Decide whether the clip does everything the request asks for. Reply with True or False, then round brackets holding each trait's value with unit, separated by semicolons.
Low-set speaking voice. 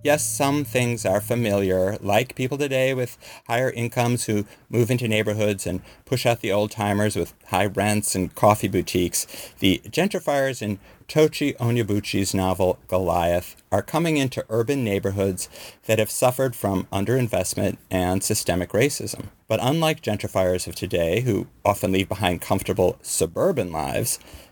True (105 Hz)